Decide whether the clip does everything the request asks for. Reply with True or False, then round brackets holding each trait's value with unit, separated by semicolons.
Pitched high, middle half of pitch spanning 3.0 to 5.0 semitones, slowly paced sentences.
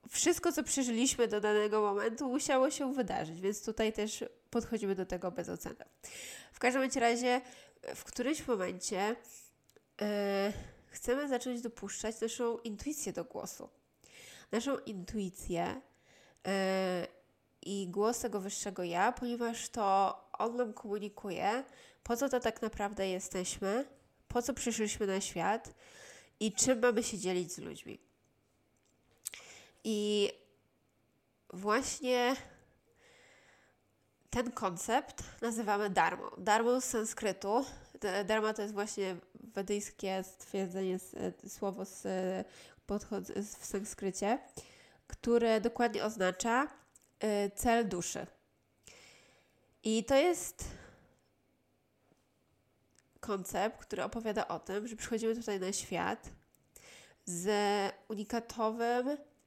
True (215 Hz; 3.5 semitones; 100 wpm)